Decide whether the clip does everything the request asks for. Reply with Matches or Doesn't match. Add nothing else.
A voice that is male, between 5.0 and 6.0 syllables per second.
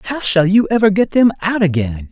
Matches